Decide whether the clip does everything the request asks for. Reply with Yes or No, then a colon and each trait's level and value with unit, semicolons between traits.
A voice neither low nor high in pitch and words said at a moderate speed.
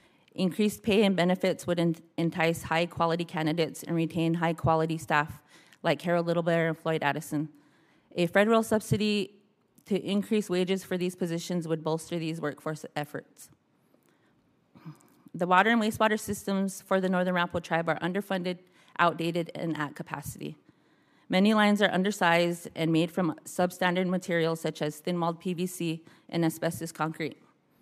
Yes: medium, 170 Hz; average, 145 wpm